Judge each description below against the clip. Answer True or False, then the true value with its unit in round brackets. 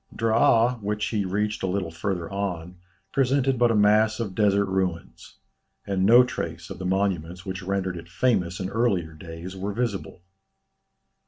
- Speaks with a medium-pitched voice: False (100 Hz)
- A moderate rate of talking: True (160 wpm)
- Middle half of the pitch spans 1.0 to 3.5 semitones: True (3.2 semitones)